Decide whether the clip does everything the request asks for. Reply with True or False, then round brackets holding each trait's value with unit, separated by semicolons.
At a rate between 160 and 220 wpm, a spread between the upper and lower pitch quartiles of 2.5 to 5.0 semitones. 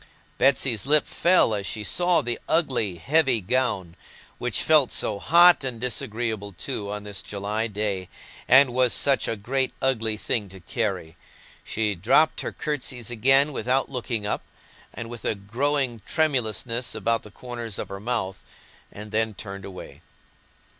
False (150 wpm; 4.4 semitones)